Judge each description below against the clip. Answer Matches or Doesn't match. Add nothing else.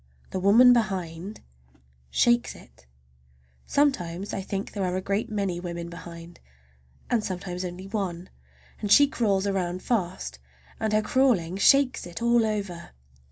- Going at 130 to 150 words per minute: Matches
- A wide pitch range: Doesn't match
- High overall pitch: Matches